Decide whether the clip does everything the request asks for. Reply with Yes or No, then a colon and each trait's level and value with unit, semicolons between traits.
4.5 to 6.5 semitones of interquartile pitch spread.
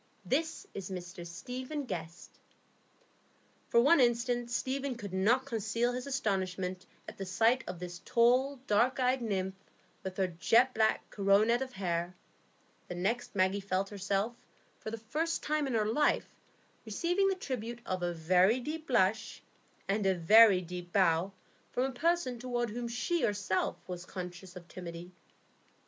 Yes: average, 5.2 semitones